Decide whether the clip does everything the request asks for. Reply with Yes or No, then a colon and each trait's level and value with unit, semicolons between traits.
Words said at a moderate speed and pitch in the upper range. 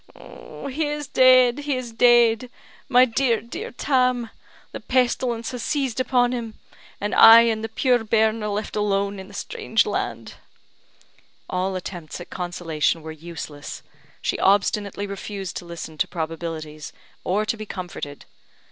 Yes: average, 145 wpm; high, 220 Hz